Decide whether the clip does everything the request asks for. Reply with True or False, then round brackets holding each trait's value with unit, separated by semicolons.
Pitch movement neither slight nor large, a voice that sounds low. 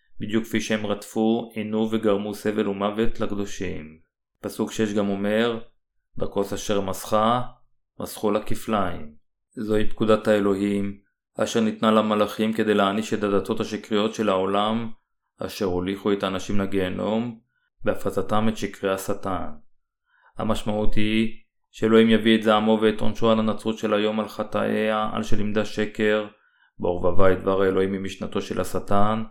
False (1.7 semitones; 105 Hz)